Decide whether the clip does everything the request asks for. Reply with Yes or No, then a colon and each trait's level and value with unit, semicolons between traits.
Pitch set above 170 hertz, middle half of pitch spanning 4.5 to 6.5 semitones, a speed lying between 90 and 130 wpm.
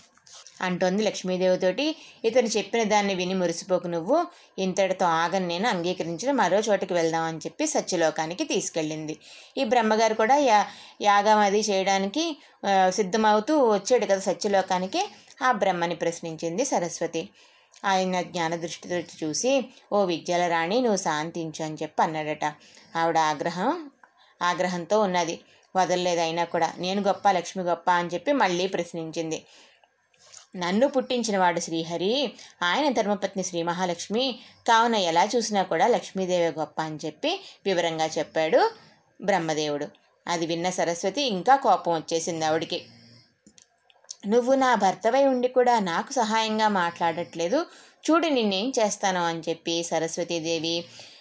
Yes: medium, 185 Hz; average, 5.0 semitones; average, 115 wpm